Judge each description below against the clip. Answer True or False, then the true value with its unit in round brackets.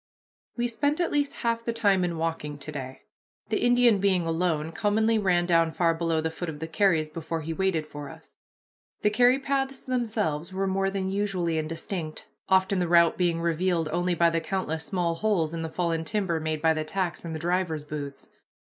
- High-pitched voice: False (175 Hz)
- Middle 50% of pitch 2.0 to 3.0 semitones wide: False (3.7 semitones)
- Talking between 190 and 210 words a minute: True (200 wpm)